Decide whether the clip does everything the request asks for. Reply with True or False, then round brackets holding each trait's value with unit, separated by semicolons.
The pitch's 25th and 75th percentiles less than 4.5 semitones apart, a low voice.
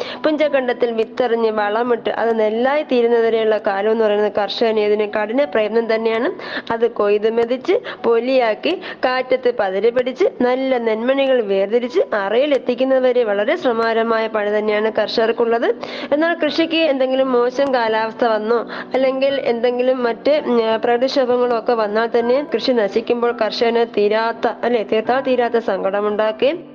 False (2.9 semitones; 235 Hz)